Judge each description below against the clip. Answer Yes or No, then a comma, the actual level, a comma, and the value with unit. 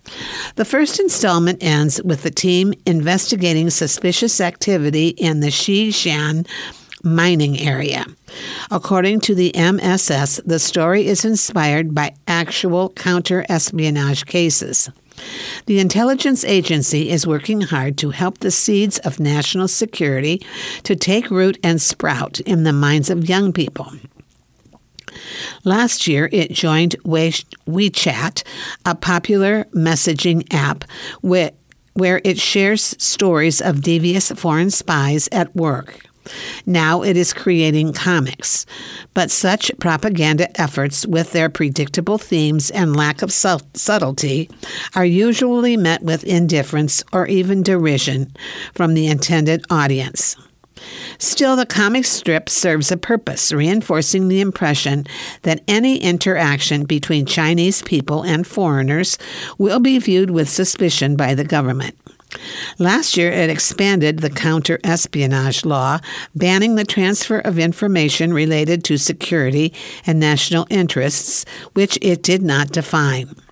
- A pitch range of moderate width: Yes, average, 3.8 semitones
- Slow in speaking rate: Yes, slow, 120 wpm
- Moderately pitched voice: Yes, medium, 170 Hz